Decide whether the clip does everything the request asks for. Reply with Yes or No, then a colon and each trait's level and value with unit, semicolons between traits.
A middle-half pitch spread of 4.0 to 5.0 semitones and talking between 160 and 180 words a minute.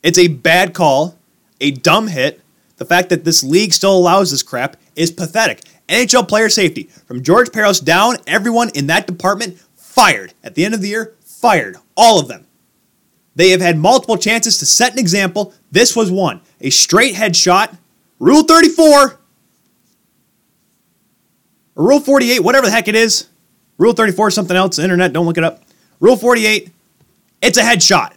Yes: average, 4.5 semitones; average, 170 wpm